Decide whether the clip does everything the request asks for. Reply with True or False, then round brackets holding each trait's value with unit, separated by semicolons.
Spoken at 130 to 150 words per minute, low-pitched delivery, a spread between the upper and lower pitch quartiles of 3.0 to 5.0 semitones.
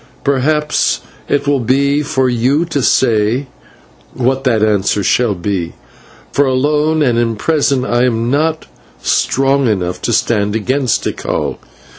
True (135 wpm; 130 Hz; 3.9 semitones)